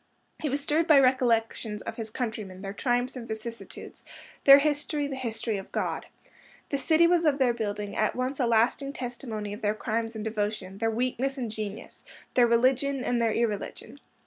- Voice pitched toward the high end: Yes, high, 235 Hz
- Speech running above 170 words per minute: Yes, average, 180 wpm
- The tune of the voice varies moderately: Yes, average, 3.7 semitones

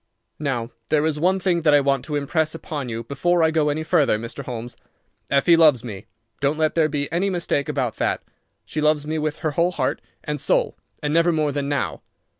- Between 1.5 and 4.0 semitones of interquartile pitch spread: Yes, narrow, 2.5 semitones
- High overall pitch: No, medium, 150 Hz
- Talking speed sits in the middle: No, fast, 215 wpm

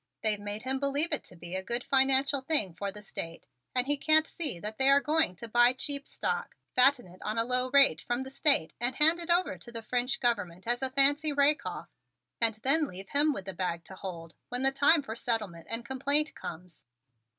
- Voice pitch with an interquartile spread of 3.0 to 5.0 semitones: No, wide, 5.5 semitones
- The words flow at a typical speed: No, fast, 225 wpm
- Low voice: No, very high, 250 Hz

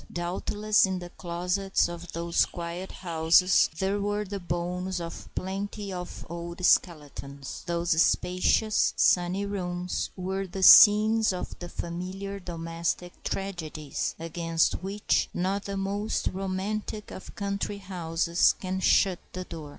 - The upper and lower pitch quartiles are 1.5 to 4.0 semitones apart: Yes, narrow, 2.4 semitones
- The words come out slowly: Yes, slow, 125 wpm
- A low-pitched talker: No, medium, 180 Hz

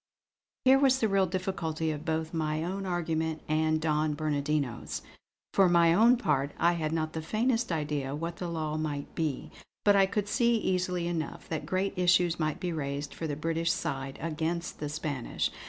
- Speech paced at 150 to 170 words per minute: No, average, 185 wpm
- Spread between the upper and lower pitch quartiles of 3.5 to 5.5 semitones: No, average, 3.0 semitones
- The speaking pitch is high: No, medium, 160 Hz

